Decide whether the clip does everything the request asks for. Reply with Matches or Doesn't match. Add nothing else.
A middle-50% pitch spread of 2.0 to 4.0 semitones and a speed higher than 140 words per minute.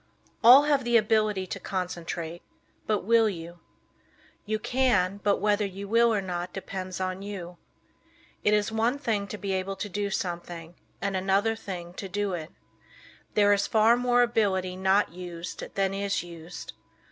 Matches